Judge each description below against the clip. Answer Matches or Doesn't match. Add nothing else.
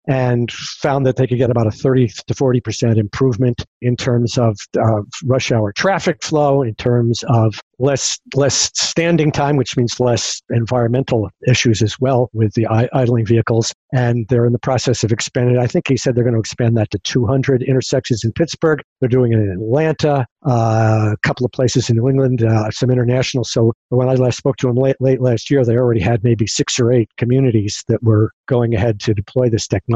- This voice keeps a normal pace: Doesn't match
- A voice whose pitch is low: Matches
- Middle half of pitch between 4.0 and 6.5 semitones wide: Doesn't match